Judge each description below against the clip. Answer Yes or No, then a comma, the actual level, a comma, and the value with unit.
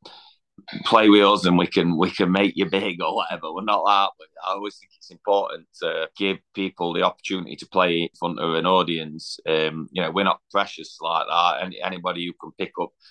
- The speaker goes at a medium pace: No, fast, 215 wpm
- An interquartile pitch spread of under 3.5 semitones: Yes, narrow, 2.5 semitones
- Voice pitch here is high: No, very low, 95 Hz